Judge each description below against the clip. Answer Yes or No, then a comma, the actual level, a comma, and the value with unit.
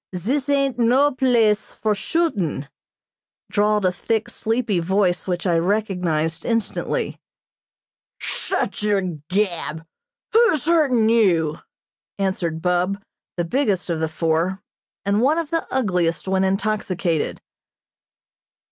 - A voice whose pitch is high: Yes, high, 200 Hz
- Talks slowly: Yes, slow, 110 wpm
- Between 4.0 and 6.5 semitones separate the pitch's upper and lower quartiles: Yes, average, 5.0 semitones